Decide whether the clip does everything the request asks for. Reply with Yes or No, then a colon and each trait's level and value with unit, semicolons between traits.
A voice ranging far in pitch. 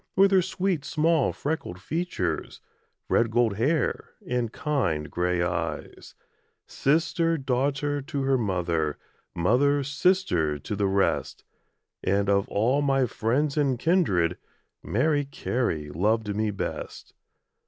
Yes: wide, 7.1 semitones